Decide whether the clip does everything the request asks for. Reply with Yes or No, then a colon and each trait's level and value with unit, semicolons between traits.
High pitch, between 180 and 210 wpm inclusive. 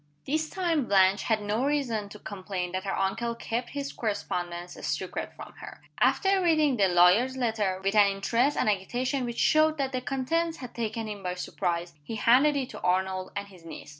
Yes: high, 220 Hz; average, 195 wpm